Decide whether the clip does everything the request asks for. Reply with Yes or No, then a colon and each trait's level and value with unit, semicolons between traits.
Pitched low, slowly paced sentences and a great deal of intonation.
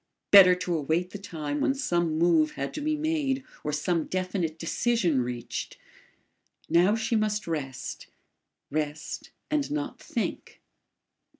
No: medium, 180 Hz; slow, 130 wpm; wide, 6.9 semitones